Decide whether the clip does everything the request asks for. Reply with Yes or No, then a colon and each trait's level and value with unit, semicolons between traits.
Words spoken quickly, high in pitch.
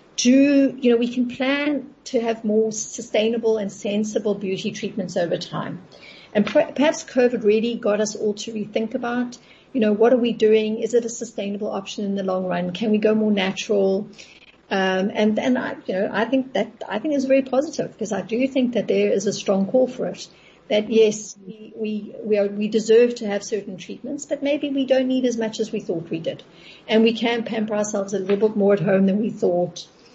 Yes: fast, 220 wpm; high, 220 Hz